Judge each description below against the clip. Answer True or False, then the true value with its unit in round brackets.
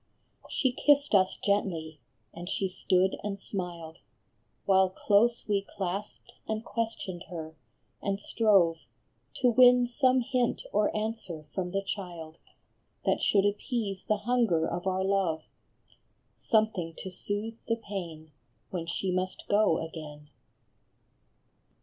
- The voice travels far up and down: False (3.9 semitones)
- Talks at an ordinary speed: False (125 wpm)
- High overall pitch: True (195 Hz)